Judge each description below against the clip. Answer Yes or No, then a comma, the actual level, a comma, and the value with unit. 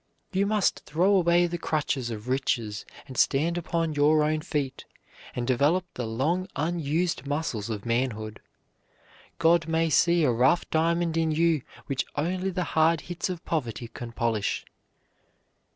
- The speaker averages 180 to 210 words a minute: No, average, 150 wpm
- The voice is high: No, medium, 155 Hz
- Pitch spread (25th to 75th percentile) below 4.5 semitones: No, average, 5.0 semitones